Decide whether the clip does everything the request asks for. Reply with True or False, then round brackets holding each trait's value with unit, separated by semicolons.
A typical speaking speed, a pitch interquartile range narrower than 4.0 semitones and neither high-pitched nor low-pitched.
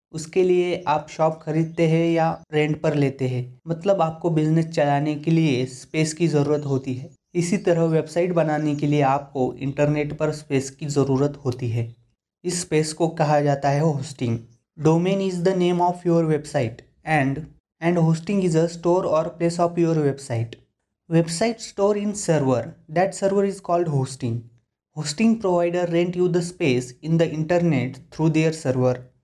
True (170 wpm; 3.6 semitones; 155 Hz)